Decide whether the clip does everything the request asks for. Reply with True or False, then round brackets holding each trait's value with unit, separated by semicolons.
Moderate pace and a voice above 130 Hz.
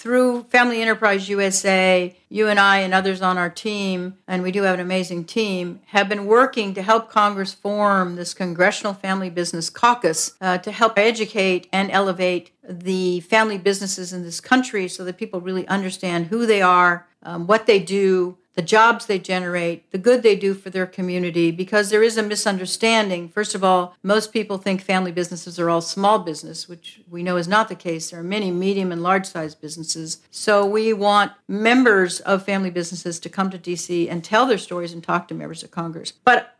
True (195 wpm; 190 Hz)